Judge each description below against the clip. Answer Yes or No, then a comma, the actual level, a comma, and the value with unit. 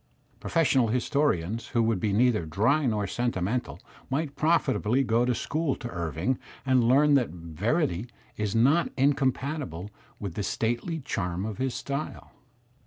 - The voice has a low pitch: Yes, low, 120 Hz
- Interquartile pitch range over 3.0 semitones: Yes, average, 5.1 semitones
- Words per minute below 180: Yes, average, 140 wpm